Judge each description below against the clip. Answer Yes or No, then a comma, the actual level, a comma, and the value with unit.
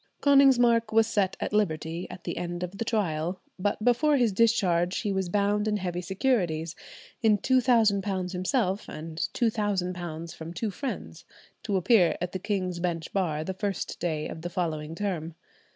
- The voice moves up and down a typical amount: Yes, average, 3.9 semitones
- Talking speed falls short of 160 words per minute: No, average, 165 wpm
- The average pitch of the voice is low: No, high, 190 Hz